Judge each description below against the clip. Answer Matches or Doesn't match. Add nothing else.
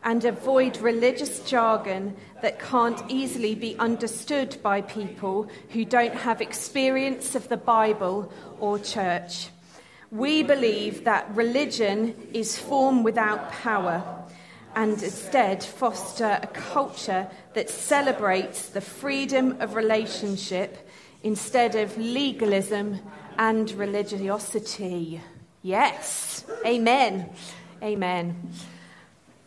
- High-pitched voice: Matches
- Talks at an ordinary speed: Doesn't match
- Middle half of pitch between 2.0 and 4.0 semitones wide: Matches